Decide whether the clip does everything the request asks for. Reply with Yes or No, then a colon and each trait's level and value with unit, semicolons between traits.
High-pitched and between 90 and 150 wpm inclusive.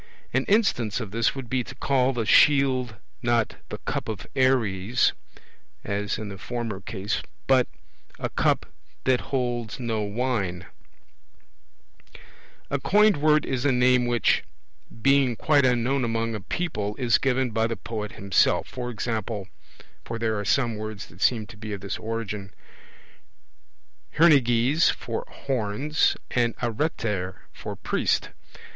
No: low, 120 Hz; average, 140 wpm